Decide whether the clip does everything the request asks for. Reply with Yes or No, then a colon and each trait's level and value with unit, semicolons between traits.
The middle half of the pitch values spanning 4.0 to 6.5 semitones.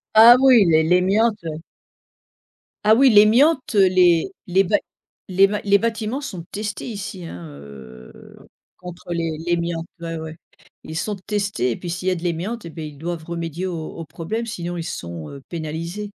Yes: average, 4.3 semitones